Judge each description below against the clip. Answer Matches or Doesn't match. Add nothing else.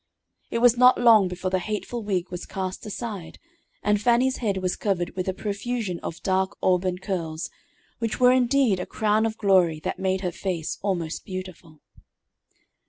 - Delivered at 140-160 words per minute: Doesn't match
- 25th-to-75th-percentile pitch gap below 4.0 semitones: Matches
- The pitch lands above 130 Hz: Matches